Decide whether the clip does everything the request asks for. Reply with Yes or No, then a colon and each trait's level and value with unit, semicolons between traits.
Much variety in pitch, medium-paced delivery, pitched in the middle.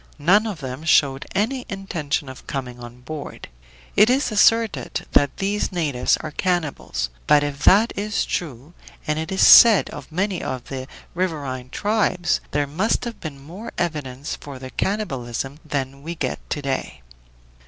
Yes: wide, 6.2 semitones; average, 160 wpm; medium, 155 Hz